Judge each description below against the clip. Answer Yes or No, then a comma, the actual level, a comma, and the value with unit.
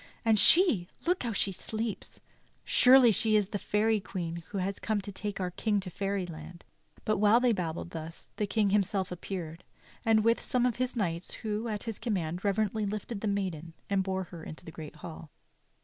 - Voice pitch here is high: Yes, high, 200 Hz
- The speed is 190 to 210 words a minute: Yes, fast, 205 wpm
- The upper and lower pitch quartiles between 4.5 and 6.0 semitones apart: No, average, 3.7 semitones